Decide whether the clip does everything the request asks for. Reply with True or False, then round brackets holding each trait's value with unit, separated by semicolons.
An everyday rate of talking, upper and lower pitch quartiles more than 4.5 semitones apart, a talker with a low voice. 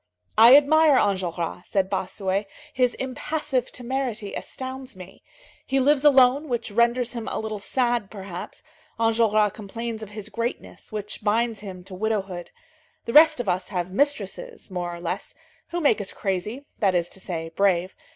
False (160 wpm; 4.9 semitones; 215 Hz)